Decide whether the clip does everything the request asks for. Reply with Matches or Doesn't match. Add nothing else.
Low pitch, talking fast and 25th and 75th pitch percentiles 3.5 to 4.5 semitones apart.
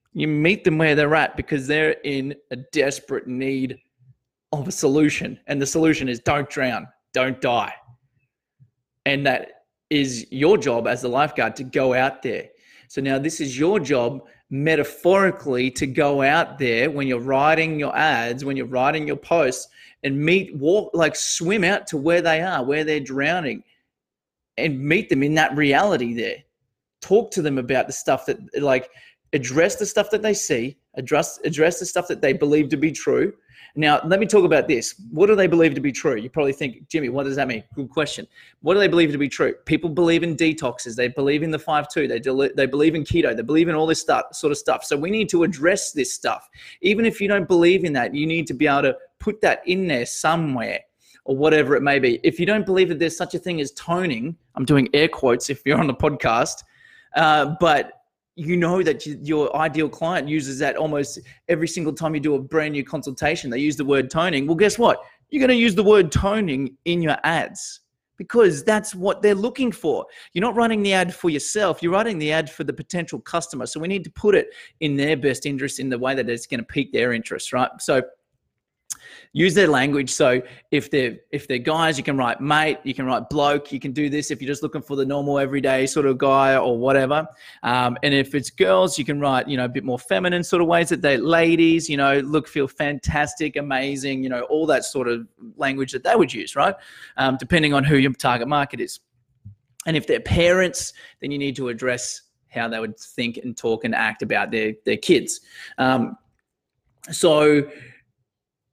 Doesn't match